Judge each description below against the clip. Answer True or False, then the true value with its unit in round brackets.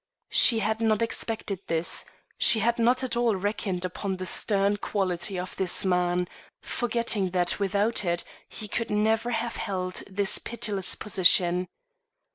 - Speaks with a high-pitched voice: True (200 Hz)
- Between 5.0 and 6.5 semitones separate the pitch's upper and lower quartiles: False (3.6 semitones)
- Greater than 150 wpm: False (145 wpm)